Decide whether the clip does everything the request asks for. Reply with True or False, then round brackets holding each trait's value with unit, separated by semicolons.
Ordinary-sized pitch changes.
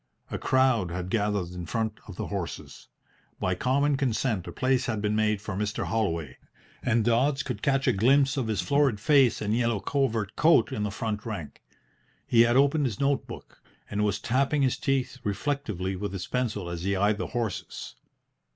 True (4.6 semitones)